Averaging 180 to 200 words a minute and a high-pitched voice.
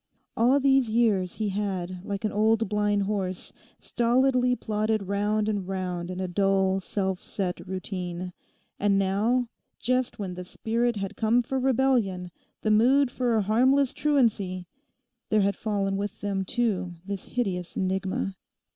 No: average, 145 wpm; high, 205 Hz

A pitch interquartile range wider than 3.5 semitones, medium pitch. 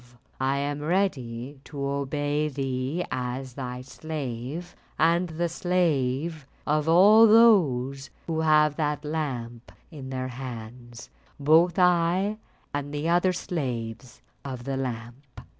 Yes: average, 4.2 semitones; medium, 145 Hz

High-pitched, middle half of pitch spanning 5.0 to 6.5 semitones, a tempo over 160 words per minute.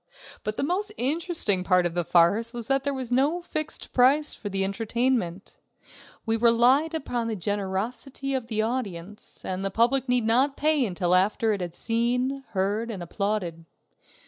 Yes: high, 230 Hz; average, 5.3 semitones; average, 170 wpm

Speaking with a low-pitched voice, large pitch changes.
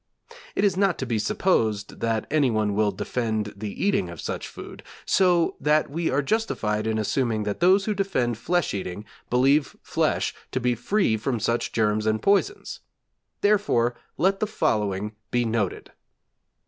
Yes: low, 120 Hz; wide, 8.7 semitones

